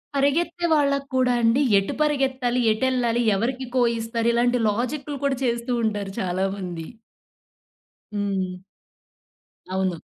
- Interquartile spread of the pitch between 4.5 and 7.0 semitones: Yes, average, 4.8 semitones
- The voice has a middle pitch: No, high, 240 Hz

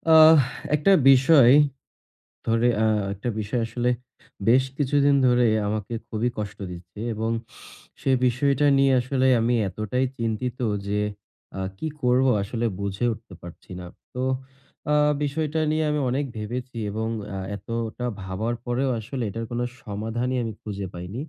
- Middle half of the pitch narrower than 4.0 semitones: Yes, average, 3.6 semitones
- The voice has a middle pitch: No, low, 120 Hz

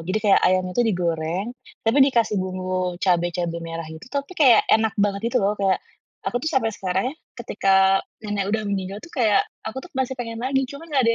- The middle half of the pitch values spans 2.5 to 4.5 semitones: No, average, 4.9 semitones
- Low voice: No, high, 205 Hz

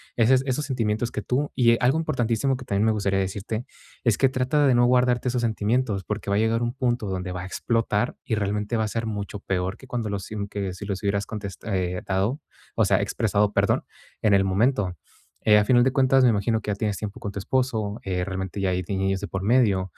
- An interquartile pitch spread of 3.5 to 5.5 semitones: Yes, average, 3.8 semitones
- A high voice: No, low, 105 Hz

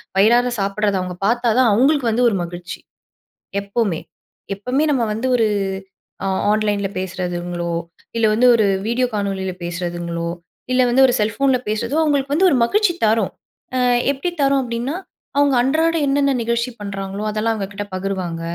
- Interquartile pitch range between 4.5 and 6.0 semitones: Yes, average, 4.8 semitones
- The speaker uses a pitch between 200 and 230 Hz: Yes, high, 220 Hz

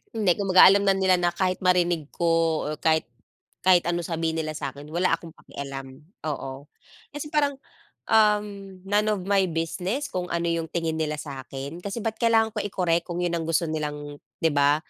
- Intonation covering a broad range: No, average, 3.7 semitones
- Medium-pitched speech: Yes, medium, 175 Hz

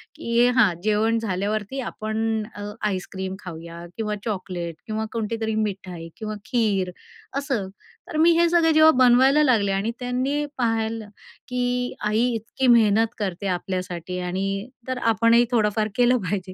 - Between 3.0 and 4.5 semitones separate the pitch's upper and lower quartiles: Yes, average, 4.0 semitones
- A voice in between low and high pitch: No, high, 220 Hz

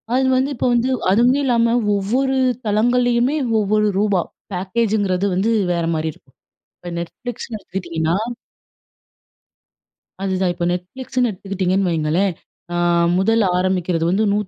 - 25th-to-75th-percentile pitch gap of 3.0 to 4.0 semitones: No, average, 4.6 semitones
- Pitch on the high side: Yes, high, 200 Hz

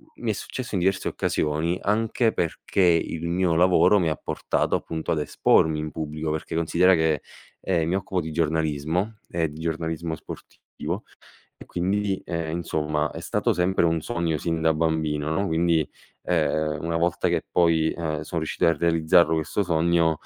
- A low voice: Yes, very low, 80 Hz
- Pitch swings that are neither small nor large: No, narrow, 2.0 semitones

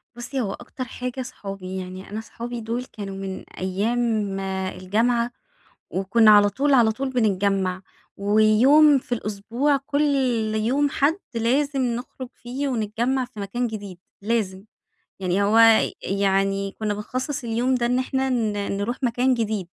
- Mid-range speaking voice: No, high, 230 Hz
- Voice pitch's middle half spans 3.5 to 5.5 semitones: Yes, average, 4.1 semitones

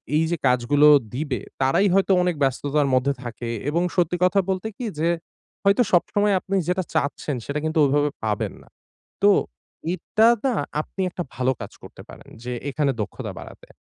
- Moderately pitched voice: Yes, medium, 155 Hz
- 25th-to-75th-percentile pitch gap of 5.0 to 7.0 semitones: Yes, wide, 5.5 semitones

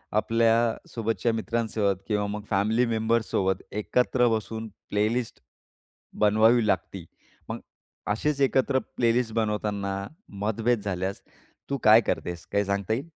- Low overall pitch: Yes, low, 110 Hz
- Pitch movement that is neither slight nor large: No, narrow, 2.2 semitones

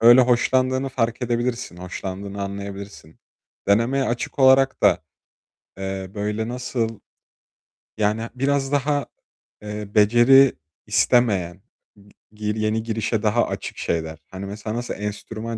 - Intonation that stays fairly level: No, average, 3.7 semitones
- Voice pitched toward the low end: Yes, low, 110 Hz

